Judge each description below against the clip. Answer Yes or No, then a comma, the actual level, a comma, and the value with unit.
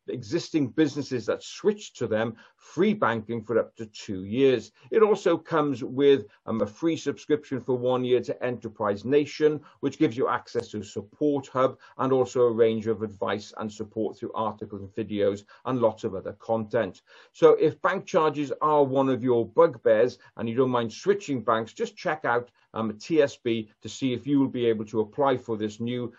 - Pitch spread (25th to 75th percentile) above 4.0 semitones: Yes, average, 4.7 semitones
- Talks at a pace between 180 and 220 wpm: Yes, average, 195 wpm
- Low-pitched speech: Yes, low, 125 Hz